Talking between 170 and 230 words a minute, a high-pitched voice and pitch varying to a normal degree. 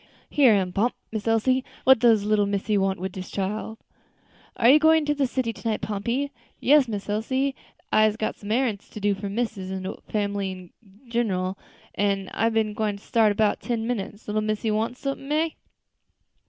Yes: average, 190 wpm; high, 215 Hz; average, 3.2 semitones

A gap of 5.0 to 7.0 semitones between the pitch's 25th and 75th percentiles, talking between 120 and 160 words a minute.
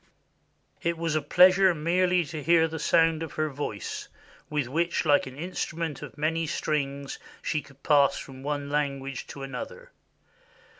No: average, 3.0 semitones; average, 155 wpm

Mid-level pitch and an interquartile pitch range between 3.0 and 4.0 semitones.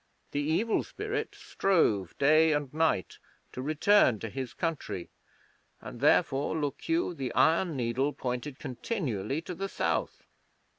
No: medium, 145 Hz; average, 4.5 semitones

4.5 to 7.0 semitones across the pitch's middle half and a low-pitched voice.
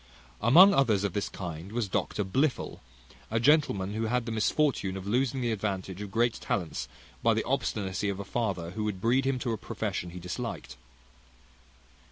No: average, 4.0 semitones; low, 105 Hz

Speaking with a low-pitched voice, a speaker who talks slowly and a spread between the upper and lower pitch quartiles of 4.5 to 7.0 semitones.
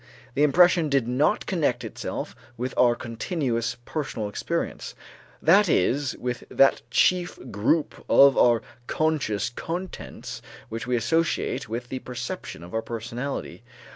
Yes: low, 125 Hz; slow, 130 wpm; average, 5.1 semitones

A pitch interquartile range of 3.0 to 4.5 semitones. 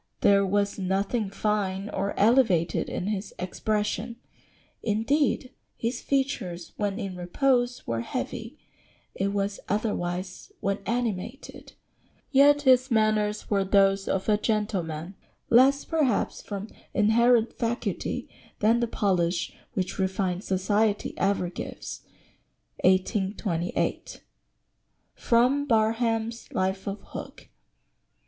Yes: average, 3.5 semitones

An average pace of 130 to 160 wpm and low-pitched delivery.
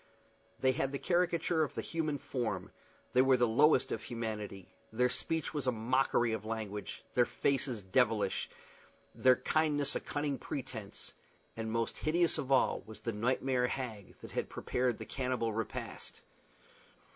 Yes: average, 150 wpm; low, 125 Hz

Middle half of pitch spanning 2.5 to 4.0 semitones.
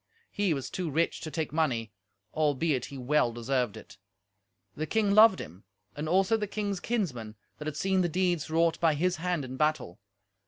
No: average, 5.1 semitones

